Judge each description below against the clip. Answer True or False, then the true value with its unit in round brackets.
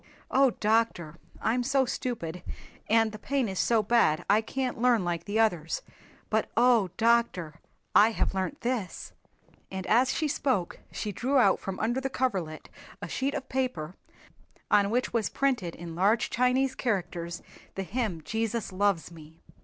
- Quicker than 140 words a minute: True (160 wpm)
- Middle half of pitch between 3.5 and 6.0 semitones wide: True (5.4 semitones)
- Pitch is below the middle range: False (220 Hz)